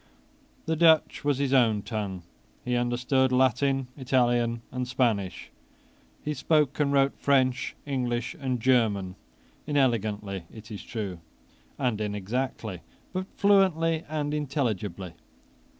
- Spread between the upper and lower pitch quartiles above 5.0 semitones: No, average, 4.4 semitones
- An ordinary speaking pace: No, slow, 115 wpm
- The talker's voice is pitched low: Yes, low, 125 Hz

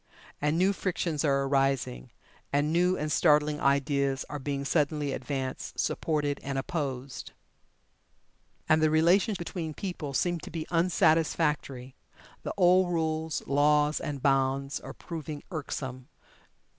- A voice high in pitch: No, medium, 150 Hz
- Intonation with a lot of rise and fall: No, average, 3.0 semitones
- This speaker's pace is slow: Yes, slow, 125 wpm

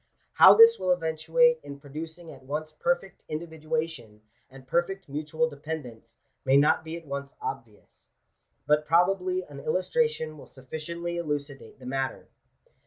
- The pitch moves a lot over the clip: No, average, 3.5 semitones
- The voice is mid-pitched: Yes, medium, 155 Hz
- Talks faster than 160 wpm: No, slow, 135 wpm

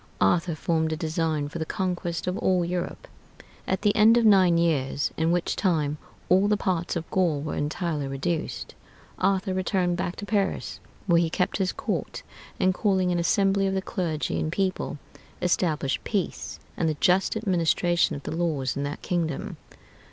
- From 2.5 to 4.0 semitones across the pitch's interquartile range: Yes, average, 3.0 semitones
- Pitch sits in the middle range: Yes, medium, 175 Hz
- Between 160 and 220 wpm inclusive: Yes, average, 175 wpm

